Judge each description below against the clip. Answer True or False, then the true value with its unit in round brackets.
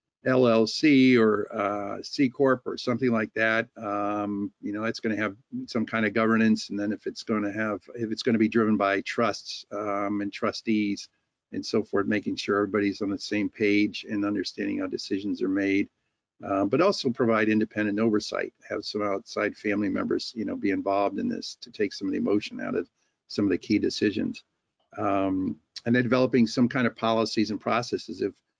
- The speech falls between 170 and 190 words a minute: False (200 wpm)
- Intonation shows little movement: True (2.0 semitones)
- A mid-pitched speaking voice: False (110 Hz)